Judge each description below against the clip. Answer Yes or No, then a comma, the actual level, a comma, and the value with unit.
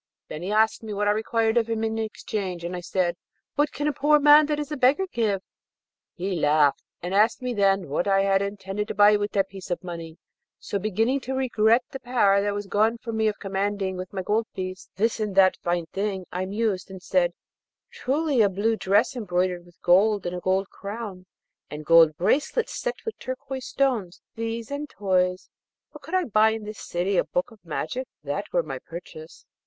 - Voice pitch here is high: Yes, high, 205 Hz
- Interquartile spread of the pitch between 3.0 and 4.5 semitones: Yes, average, 3.8 semitones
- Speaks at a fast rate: Yes, fast, 210 wpm